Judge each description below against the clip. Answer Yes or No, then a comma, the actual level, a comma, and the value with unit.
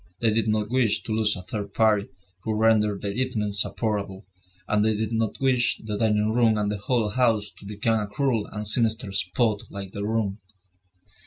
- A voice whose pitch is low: Yes, low, 110 Hz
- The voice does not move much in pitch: Yes, narrow, 1.6 semitones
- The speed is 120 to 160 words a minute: No, average, 190 wpm